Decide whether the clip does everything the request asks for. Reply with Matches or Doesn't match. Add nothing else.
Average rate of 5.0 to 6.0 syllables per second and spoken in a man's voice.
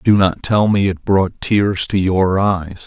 Doesn't match